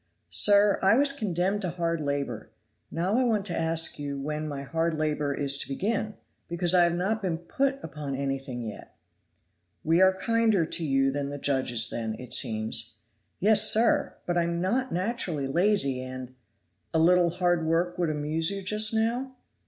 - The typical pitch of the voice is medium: Yes, medium, 170 Hz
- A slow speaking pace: No, average, 180 wpm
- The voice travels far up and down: Yes, wide, 5.9 semitones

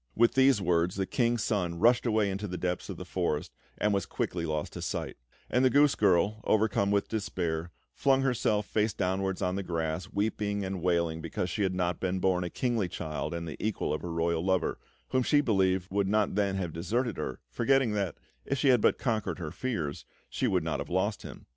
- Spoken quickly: Yes, fast, 215 wpm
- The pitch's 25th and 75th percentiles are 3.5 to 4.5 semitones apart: Yes, average, 3.9 semitones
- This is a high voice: No, very low, 95 Hz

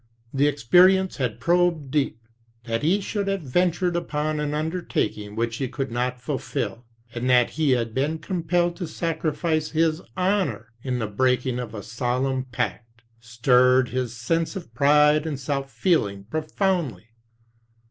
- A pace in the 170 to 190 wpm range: No, average, 145 wpm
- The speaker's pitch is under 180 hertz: Yes, medium, 140 Hz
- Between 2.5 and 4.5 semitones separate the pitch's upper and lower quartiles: No, average, 5.3 semitones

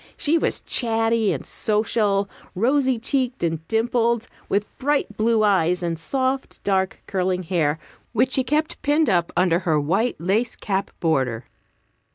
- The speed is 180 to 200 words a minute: No, average, 145 wpm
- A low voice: No, high, 215 Hz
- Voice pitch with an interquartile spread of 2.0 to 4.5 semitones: No, wide, 5.5 semitones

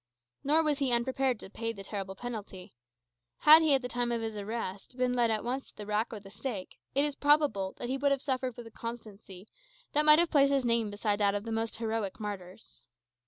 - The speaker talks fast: Yes, fast, 225 wpm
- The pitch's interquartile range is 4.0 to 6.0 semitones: Yes, average, 4.4 semitones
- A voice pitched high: Yes, high, 230 Hz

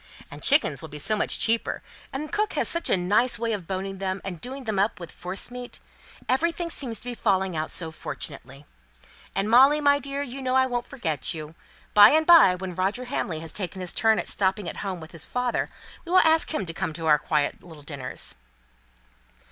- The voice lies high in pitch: Yes, high, 200 Hz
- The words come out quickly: Yes, fast, 210 wpm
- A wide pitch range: Yes, wide, 6.9 semitones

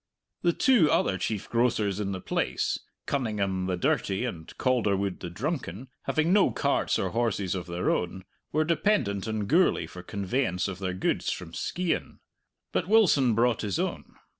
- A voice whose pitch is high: No, low, 105 Hz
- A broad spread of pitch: Yes, wide, 6.3 semitones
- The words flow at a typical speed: Yes, average, 165 wpm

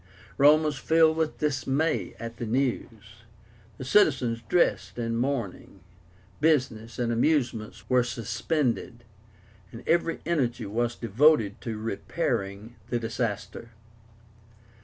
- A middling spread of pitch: Yes, average, 4.4 semitones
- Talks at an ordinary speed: No, slow, 110 wpm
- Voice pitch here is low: Yes, low, 120 Hz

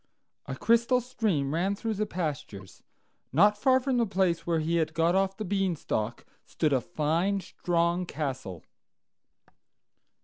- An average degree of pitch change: Yes, average, 5.0 semitones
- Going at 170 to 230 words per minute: No, average, 140 wpm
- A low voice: No, medium, 175 Hz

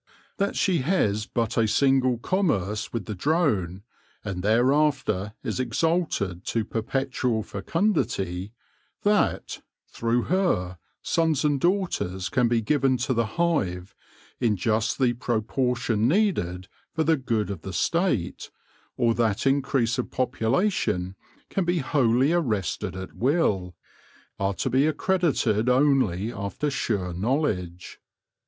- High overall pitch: No, low, 120 Hz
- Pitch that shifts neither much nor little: No, wide, 6.5 semitones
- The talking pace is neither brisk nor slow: No, slow, 125 wpm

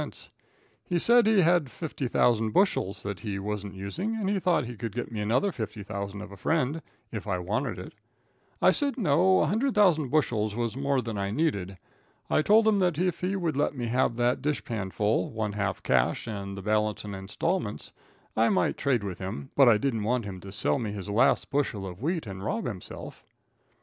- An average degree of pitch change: No, wide, 7.9 semitones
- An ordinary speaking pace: Yes, average, 195 wpm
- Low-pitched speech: Yes, low, 115 Hz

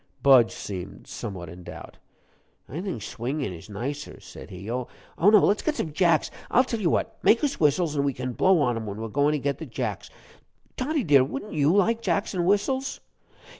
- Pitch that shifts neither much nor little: No, wide, 8.5 semitones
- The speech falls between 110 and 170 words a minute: No, fast, 205 wpm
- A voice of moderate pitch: Yes, medium, 145 Hz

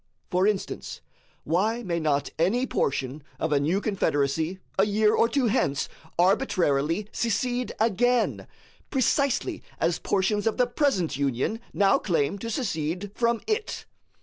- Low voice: No, high, 200 Hz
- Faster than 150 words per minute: No, slow, 135 wpm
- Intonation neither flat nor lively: No, wide, 6.5 semitones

